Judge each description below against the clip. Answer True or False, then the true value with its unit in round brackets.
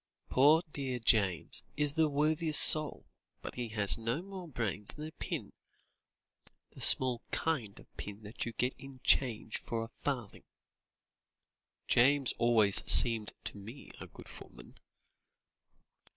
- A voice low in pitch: True (125 Hz)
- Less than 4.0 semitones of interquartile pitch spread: False (4.8 semitones)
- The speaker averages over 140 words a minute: False (135 wpm)